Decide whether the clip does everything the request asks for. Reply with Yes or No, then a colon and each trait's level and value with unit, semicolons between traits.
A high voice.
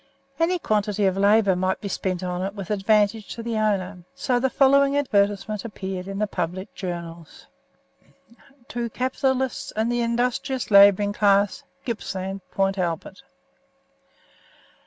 Yes: high, 205 Hz